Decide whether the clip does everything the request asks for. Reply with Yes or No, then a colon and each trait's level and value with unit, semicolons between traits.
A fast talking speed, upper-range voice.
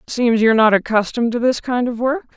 Yes: fast, 230 wpm; high, 235 Hz